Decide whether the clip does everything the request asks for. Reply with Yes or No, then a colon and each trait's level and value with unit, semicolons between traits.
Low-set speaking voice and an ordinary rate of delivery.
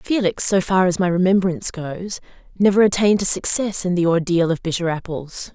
No: medium, 185 Hz; average, 185 wpm